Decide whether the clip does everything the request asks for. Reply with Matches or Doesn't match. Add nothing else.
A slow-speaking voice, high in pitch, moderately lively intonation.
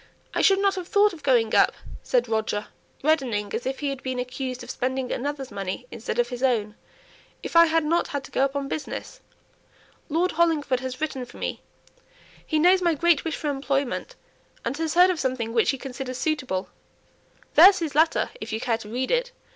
Doesn't match